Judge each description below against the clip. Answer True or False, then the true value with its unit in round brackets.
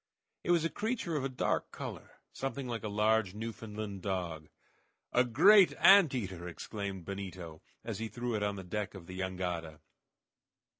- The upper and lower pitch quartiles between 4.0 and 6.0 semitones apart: True (5.2 semitones)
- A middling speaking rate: True (165 wpm)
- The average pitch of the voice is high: False (105 Hz)